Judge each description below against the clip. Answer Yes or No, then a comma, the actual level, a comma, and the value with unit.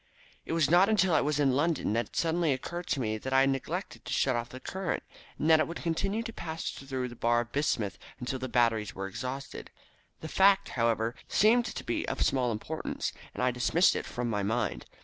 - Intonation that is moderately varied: No, wide, 5.9 semitones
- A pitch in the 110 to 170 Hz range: Yes, low, 135 Hz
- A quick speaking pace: Yes, fast, 225 wpm